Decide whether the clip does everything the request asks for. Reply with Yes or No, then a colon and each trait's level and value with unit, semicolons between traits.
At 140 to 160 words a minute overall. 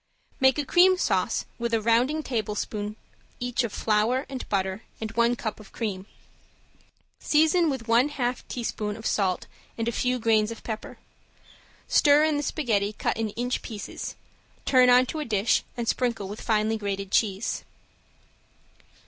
Yes: average, 155 wpm